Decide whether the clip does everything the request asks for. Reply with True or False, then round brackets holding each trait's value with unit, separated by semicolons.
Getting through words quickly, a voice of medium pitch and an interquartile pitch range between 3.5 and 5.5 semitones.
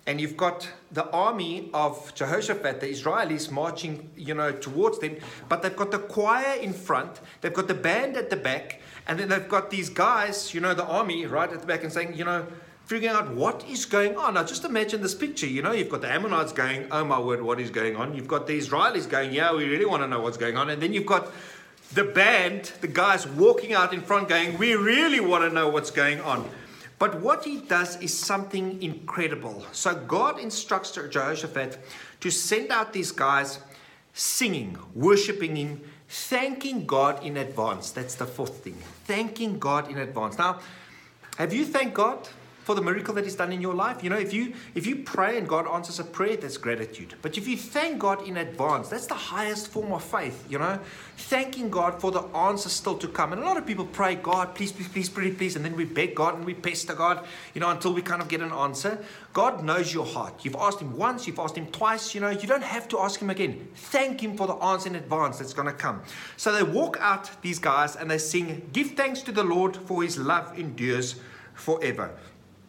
True (220 wpm; 175 Hz; 4.9 semitones)